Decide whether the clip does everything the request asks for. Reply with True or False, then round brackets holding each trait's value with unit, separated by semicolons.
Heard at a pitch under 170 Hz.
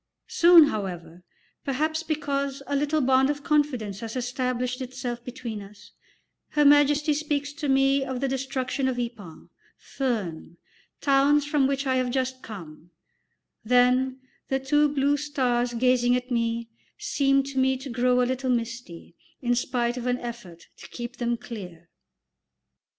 False (255 Hz)